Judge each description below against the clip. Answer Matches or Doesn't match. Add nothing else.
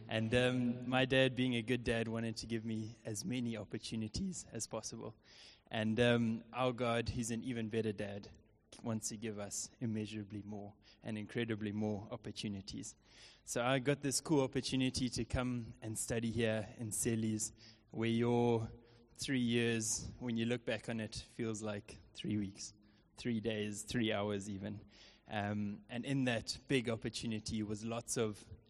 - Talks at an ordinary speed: Matches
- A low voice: Matches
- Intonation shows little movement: Matches